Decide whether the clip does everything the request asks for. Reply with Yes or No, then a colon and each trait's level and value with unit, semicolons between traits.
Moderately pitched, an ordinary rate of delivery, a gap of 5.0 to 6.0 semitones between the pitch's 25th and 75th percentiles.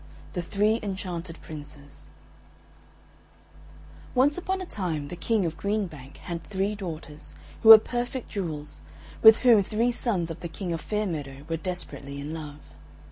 Yes: medium, 180 Hz; average, 160 wpm; wide, 5.5 semitones